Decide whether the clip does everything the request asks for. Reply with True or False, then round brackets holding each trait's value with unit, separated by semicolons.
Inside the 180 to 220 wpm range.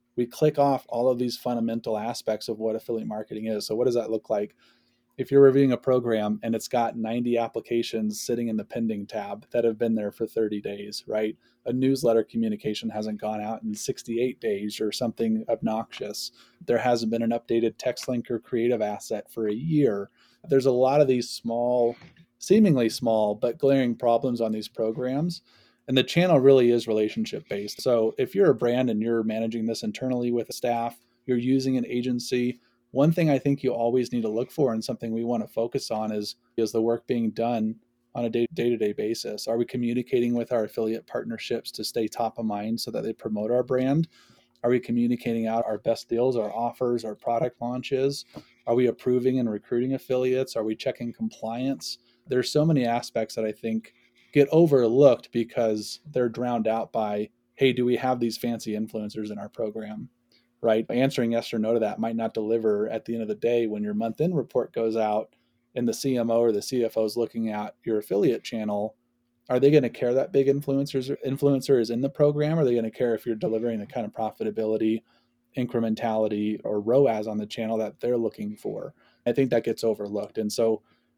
True (200 wpm)